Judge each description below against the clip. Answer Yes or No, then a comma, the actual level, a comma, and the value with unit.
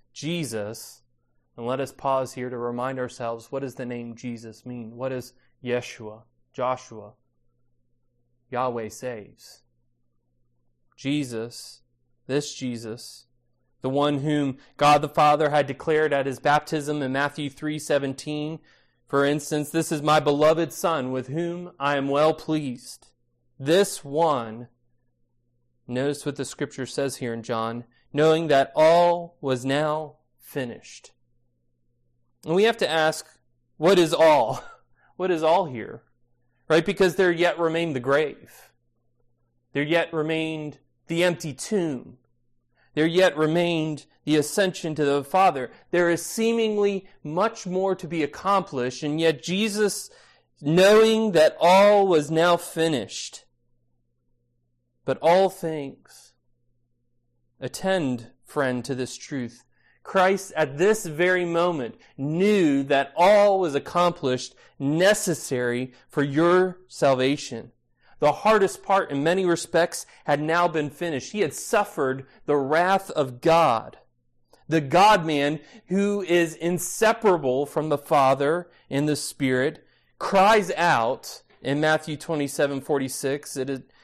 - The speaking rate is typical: No, slow, 125 wpm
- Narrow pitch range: No, average, 5.3 semitones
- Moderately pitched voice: Yes, medium, 145 Hz